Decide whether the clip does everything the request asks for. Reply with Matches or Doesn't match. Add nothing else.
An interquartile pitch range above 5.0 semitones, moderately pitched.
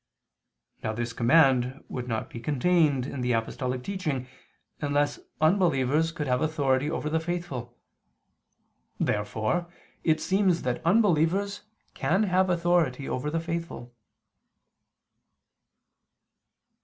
Matches